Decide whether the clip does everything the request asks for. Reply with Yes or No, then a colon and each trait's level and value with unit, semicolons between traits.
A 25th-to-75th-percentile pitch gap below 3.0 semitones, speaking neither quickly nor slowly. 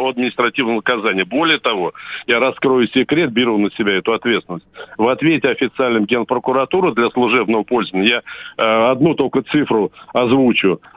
Yes: narrow, 2.6 semitones; average, 135 wpm